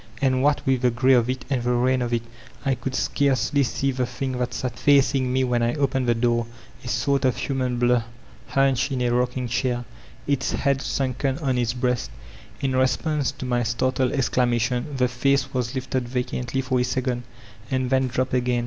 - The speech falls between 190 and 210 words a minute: Yes, average, 200 wpm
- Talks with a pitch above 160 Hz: No, low, 130 Hz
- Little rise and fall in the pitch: Yes, narrow, 1.5 semitones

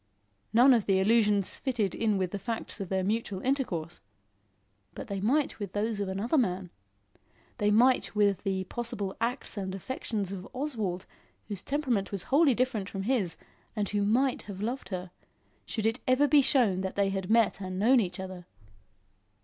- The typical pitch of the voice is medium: No, high, 205 Hz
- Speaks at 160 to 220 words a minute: Yes, average, 175 wpm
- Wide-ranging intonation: No, average, 4.0 semitones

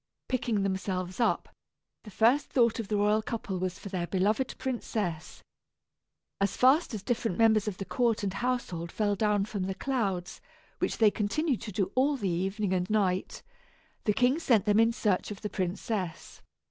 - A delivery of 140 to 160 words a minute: No, average, 175 wpm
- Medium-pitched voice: No, high, 210 Hz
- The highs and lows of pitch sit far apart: No, average, 3.5 semitones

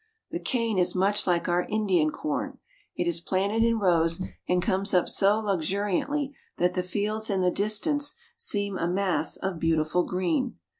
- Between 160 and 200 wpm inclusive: Yes, average, 165 wpm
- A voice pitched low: No, high, 190 Hz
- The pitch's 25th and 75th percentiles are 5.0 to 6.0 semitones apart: No, average, 3.2 semitones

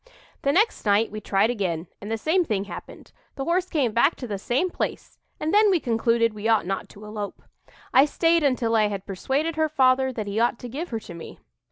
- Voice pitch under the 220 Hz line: No, high, 235 Hz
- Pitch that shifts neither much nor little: No, wide, 6.2 semitones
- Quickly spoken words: Yes, fast, 225 wpm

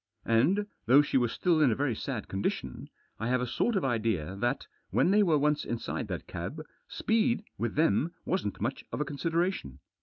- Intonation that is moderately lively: No, wide, 6.8 semitones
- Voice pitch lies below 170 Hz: Yes, medium, 140 Hz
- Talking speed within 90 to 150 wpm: No, average, 190 wpm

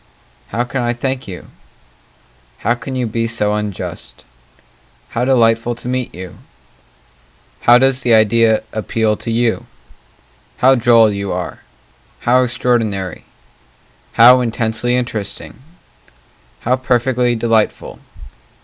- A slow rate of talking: Yes, slow, 115 wpm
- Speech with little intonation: Yes, narrow, 2.0 semitones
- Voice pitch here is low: Yes, low, 120 Hz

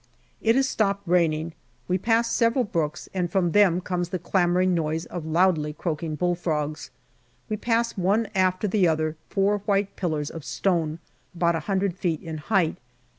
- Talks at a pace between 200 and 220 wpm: No, average, 170 wpm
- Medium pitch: Yes, medium, 180 Hz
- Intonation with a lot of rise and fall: No, average, 3.6 semitones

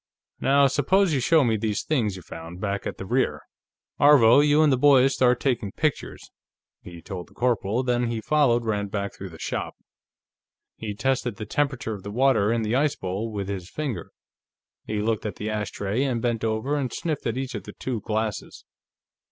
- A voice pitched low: Yes, low, 115 Hz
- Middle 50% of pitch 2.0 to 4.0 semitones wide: No, average, 4.5 semitones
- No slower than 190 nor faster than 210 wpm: Yes, average, 195 wpm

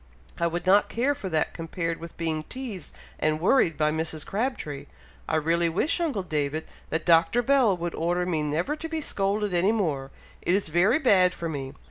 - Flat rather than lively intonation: No, average, 4.6 semitones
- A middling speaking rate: Yes, average, 190 wpm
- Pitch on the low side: No, medium, 175 Hz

